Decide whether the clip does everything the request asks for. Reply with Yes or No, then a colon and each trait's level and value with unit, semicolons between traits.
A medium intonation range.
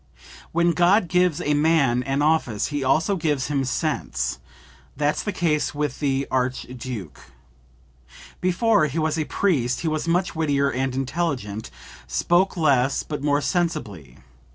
Yes: average, 4.1 semitones